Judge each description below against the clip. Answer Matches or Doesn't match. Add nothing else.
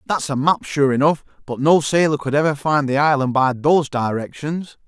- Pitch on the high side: Doesn't match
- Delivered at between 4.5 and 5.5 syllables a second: Matches